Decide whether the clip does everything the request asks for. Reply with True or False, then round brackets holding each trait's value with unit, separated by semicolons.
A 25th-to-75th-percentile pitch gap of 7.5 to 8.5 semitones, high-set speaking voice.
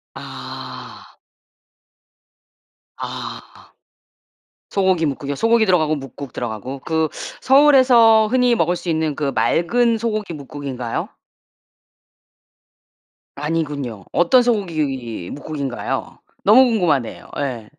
False (8.0 semitones; 160 Hz)